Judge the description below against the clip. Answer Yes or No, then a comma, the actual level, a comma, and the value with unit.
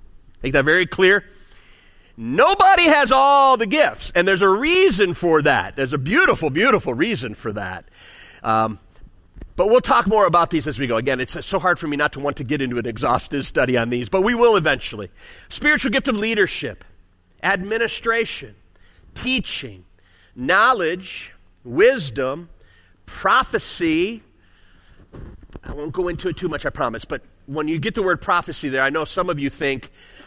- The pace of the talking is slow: No, average, 170 wpm